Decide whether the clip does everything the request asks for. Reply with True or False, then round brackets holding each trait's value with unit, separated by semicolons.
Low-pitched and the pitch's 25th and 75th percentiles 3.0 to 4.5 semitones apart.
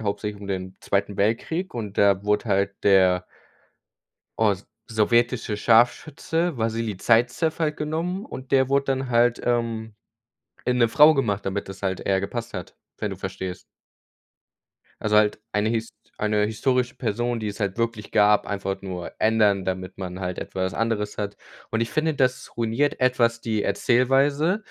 True (110 Hz; 3.9 semitones)